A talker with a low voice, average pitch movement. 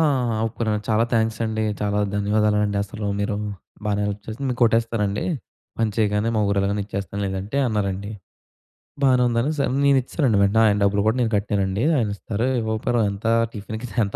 No: low, 105 Hz; narrow, 2.0 semitones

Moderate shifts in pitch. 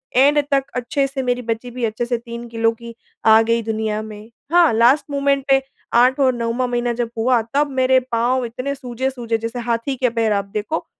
No: narrow, 2.3 semitones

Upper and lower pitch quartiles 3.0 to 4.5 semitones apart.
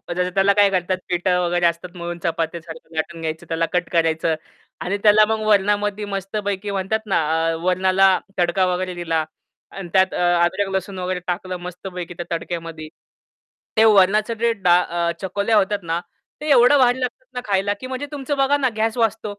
Yes: average, 3.3 semitones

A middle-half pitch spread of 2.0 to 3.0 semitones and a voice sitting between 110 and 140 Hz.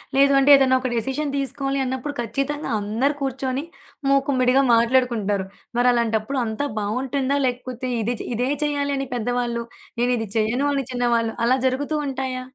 No: narrow, 2.6 semitones; very high, 255 Hz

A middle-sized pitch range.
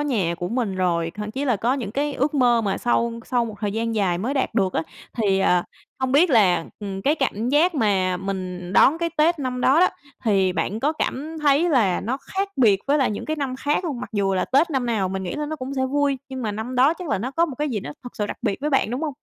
No: wide, 6.2 semitones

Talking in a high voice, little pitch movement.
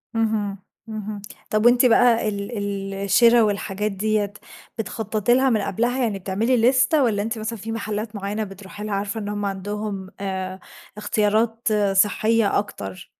Yes: high, 210 Hz; narrow, 2.2 semitones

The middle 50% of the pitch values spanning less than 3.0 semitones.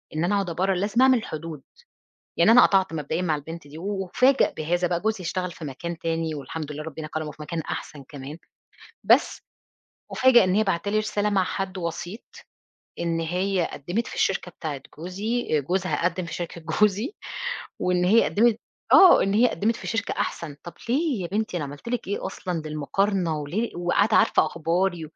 No: average, 4.1 semitones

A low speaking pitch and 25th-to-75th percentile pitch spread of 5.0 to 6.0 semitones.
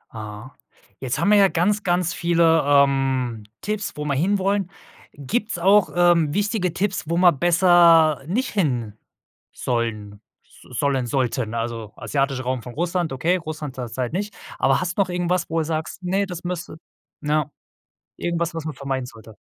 No: medium, 160 Hz; wide, 5.5 semitones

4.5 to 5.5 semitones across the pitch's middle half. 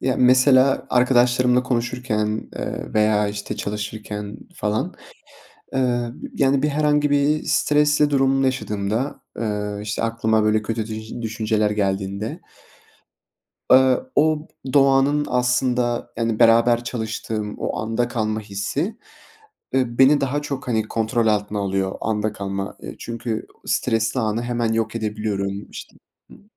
No: average, 3.4 semitones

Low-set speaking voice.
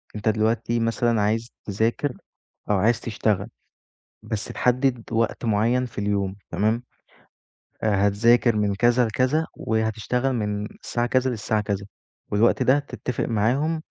Yes: low, 115 Hz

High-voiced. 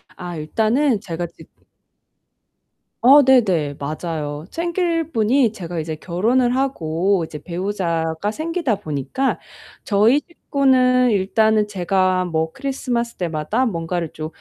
Yes: high, 200 Hz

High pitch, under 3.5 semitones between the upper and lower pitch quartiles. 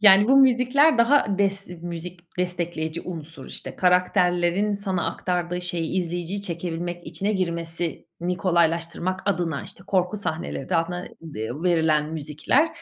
No: medium, 175 Hz; narrow, 2.5 semitones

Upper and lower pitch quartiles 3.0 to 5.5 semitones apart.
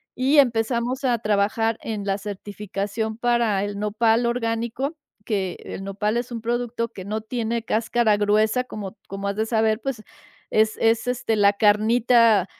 No: narrow, 2.4 semitones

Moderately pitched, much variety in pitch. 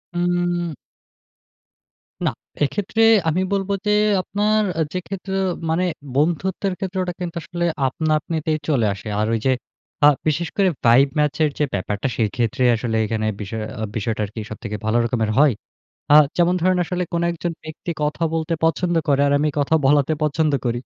Yes: medium, 155 Hz; wide, 6.3 semitones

